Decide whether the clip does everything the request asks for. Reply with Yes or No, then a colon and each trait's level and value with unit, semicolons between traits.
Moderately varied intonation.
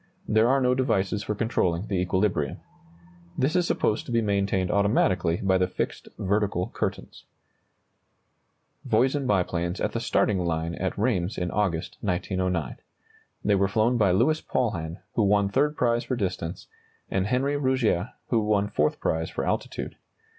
Yes: average, 4.4 semitones